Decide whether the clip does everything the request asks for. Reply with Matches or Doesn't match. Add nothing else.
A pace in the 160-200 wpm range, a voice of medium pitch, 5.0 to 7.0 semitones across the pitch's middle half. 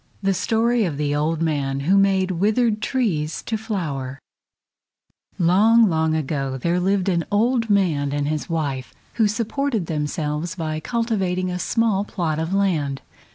Doesn't match